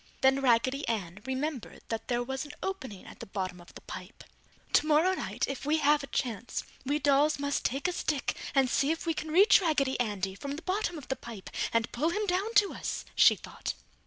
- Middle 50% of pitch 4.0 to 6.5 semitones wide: Yes, average, 4.7 semitones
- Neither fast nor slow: No, fast, 215 wpm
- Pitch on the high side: Yes, very high, 275 Hz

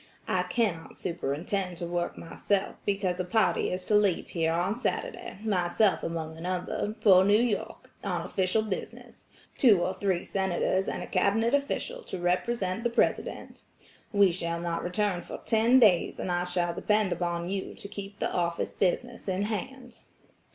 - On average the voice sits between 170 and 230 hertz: Yes, high, 190 Hz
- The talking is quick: No, average, 165 wpm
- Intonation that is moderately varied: Yes, average, 3.3 semitones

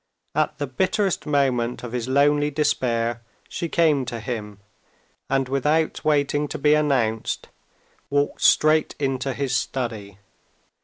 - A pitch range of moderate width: Yes, average, 3.4 semitones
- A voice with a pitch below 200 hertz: Yes, low, 135 Hz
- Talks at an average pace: No, slow, 125 wpm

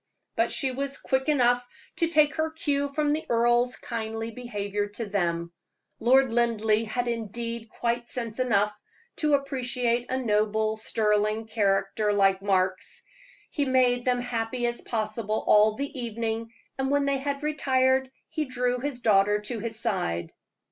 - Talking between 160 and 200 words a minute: No, average, 150 wpm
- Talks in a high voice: Yes, high, 235 Hz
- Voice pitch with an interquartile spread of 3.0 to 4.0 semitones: Yes, average, 3.4 semitones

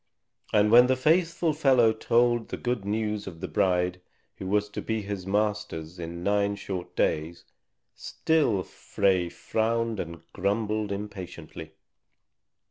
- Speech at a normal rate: No, slow, 130 wpm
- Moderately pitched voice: No, low, 105 Hz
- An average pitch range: Yes, average, 3.9 semitones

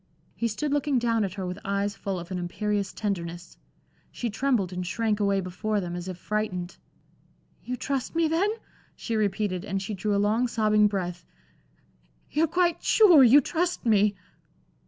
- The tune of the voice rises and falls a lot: No, average, 4.7 semitones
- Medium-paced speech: Yes, average, 170 wpm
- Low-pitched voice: No, high, 210 Hz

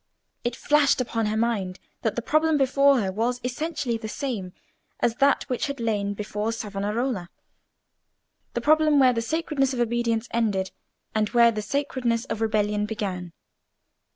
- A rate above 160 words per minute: No, average, 150 wpm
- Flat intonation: No, average, 4.1 semitones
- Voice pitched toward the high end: Yes, high, 230 Hz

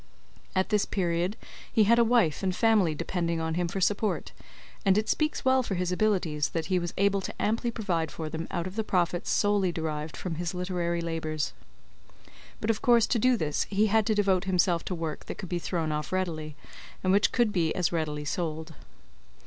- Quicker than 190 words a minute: Yes, fast, 205 wpm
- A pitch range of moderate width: Yes, average, 4.0 semitones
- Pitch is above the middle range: No, medium, 180 Hz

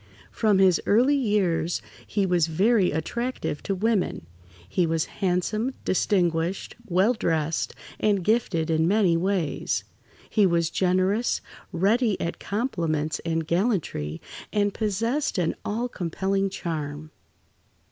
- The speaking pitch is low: No, medium, 185 Hz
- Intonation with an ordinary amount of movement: Yes, average, 4.3 semitones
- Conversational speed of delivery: No, slow, 115 wpm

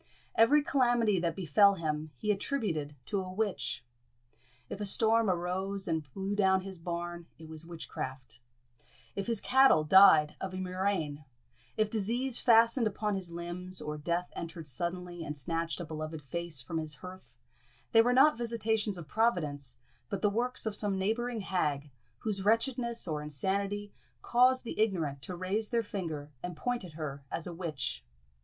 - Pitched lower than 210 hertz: Yes, medium, 185 Hz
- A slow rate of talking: No, average, 165 wpm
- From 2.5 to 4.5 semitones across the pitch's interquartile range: No, average, 5.2 semitones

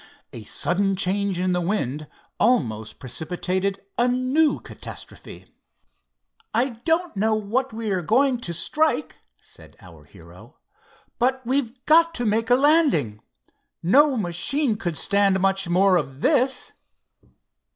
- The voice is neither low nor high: No, high, 210 Hz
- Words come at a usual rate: No, slow, 130 wpm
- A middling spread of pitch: No, wide, 6.2 semitones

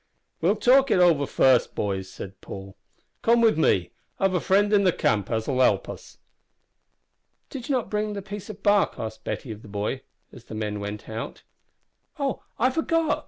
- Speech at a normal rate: Yes, average, 185 wpm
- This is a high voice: No, medium, 180 Hz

